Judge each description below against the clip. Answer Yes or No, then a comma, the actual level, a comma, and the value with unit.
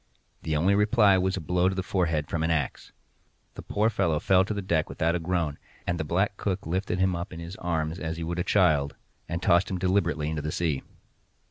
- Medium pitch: No, very low, 85 Hz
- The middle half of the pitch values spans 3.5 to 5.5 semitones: No, average, 2.9 semitones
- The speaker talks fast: Yes, fast, 230 wpm